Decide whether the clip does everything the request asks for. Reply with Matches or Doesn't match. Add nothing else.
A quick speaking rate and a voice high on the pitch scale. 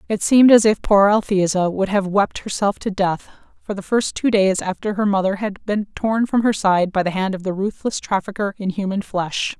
Matches